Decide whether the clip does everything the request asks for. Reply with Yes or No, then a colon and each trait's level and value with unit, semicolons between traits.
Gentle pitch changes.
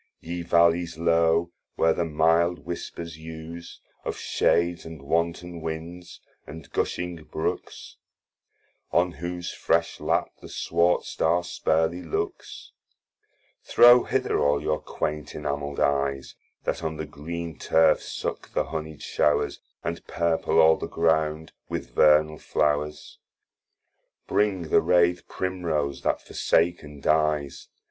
Yes: narrow, 2.0 semitones